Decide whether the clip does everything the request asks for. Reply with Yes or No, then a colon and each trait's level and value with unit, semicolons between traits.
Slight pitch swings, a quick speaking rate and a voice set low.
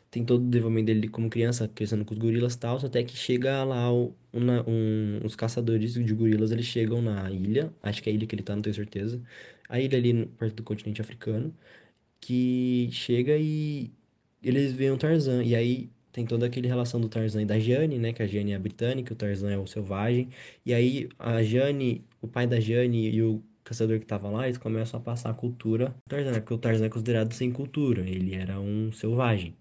Yes: narrow, 2.1 semitones; fast, 220 wpm; low, 115 Hz